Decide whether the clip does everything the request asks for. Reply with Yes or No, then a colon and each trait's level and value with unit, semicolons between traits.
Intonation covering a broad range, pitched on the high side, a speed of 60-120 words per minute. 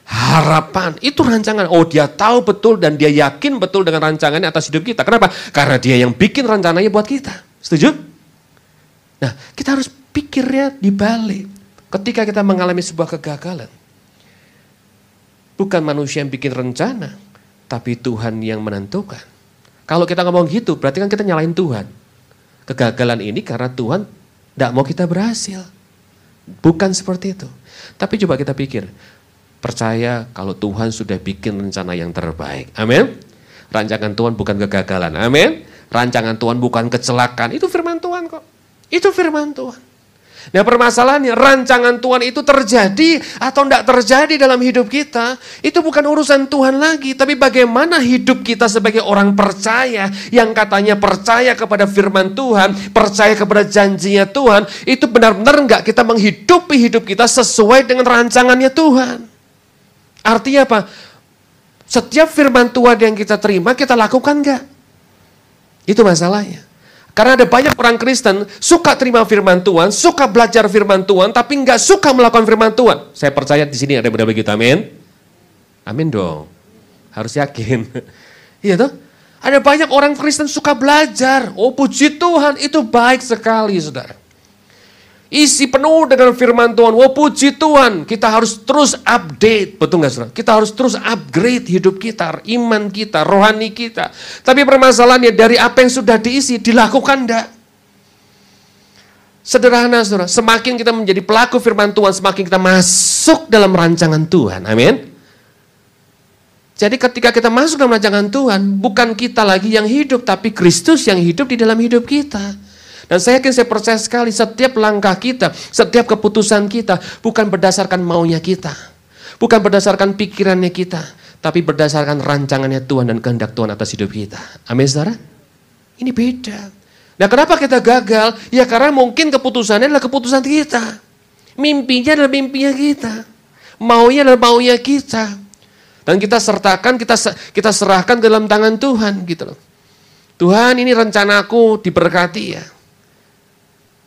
No: wide, 7.0 semitones; high, 215 Hz; fast, 140 wpm